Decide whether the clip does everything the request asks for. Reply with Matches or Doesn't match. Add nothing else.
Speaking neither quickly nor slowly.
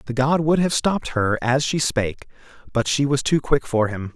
Doesn't match